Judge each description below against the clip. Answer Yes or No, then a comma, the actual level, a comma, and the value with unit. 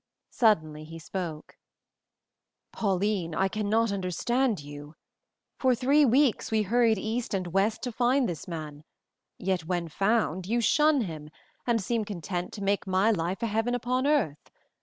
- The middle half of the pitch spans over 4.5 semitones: Yes, average, 5.3 semitones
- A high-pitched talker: Yes, high, 205 Hz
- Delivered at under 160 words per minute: Yes, average, 150 wpm